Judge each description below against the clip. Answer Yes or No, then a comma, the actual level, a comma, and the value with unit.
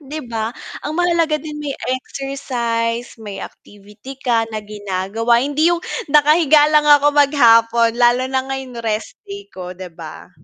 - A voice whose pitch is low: No, very high, 250 Hz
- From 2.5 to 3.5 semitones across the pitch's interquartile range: No, average, 4.6 semitones